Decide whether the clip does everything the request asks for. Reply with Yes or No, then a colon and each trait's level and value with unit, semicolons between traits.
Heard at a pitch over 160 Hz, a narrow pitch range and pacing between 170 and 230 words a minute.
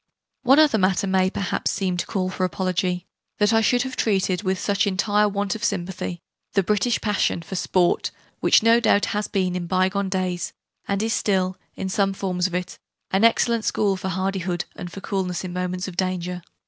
Yes: high, 190 Hz; narrow, 2.1 semitones; average, 200 wpm